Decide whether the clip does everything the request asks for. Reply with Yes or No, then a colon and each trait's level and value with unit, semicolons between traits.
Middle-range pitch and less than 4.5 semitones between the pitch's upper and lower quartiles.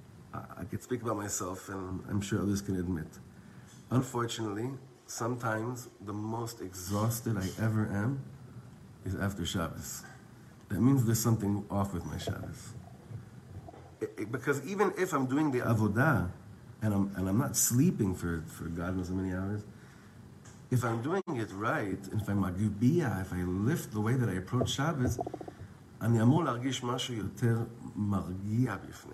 No: low, 110 Hz; average, 4.0 semitones